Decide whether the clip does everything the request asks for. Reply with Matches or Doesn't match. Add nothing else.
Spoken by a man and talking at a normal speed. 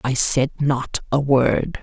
Doesn't match